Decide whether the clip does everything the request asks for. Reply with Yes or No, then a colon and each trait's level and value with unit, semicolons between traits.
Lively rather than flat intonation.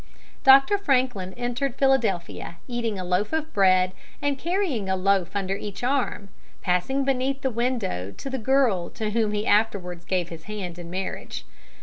Yes: wide, 6.2 semitones